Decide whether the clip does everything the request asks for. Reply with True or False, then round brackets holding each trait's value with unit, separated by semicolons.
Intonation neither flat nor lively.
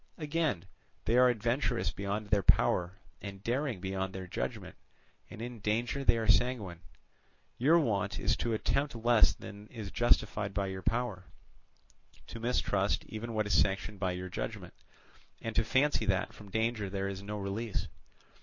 True (3.3 semitones)